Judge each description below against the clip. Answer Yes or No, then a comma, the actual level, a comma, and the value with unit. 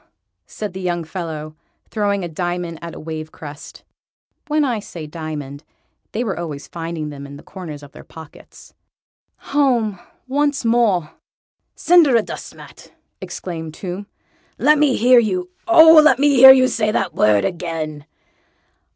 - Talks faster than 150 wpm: No, average, 140 wpm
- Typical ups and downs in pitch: No, wide, 7.5 semitones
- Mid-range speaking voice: Yes, medium, 180 Hz